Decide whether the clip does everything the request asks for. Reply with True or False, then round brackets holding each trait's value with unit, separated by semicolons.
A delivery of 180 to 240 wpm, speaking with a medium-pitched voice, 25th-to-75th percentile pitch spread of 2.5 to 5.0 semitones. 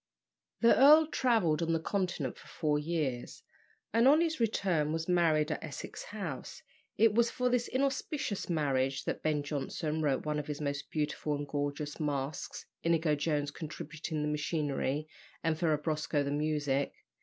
False (155 wpm; 155 Hz; 3.5 semitones)